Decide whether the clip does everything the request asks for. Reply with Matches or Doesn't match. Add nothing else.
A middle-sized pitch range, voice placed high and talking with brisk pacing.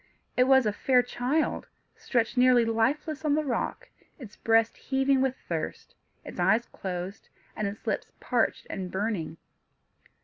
Doesn't match